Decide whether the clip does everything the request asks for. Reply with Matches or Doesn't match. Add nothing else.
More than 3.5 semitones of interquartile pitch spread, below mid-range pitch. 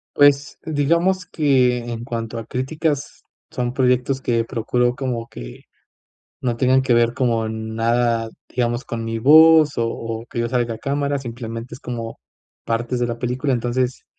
Doesn't match